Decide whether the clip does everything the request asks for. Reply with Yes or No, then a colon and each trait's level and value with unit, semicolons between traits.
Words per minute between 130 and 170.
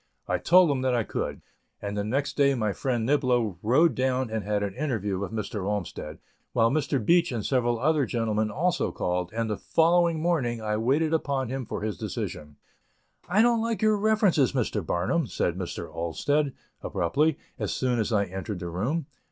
No: average, 185 wpm